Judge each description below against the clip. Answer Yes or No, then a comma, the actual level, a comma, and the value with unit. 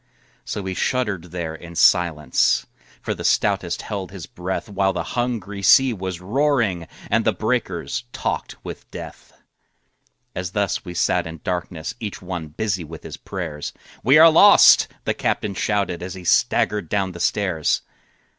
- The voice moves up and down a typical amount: Yes, average, 3.1 semitones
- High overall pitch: No, very low, 95 Hz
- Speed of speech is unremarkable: Yes, average, 155 wpm